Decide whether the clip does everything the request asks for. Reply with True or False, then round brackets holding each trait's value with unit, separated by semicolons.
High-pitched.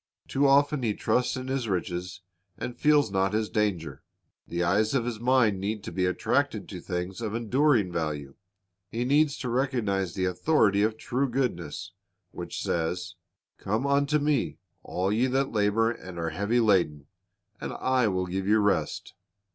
False (105 Hz)